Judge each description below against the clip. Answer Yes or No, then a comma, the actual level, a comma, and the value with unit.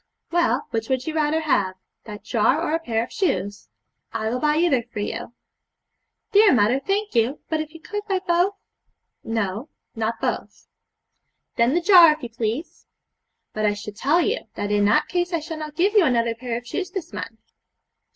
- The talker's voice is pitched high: Yes, very high, 280 Hz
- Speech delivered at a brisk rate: No, average, 190 wpm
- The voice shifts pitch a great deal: Yes, wide, 7.2 semitones